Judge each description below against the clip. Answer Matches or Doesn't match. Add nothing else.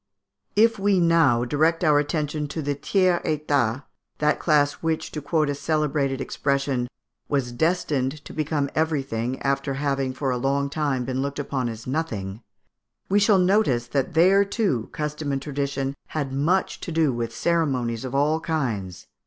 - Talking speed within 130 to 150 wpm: Doesn't match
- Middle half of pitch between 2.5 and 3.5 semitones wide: Matches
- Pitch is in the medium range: Matches